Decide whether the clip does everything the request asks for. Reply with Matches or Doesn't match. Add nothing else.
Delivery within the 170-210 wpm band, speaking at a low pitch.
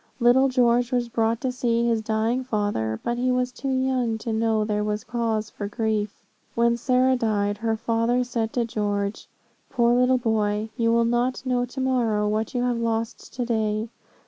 Doesn't match